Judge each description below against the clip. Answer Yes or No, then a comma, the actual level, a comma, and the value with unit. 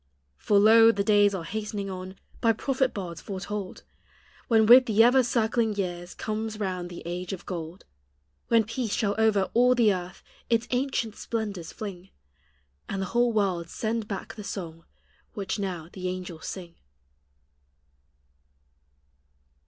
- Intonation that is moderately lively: Yes, average, 3.5 semitones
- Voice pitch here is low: No, high, 205 Hz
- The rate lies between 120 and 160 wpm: Yes, average, 145 wpm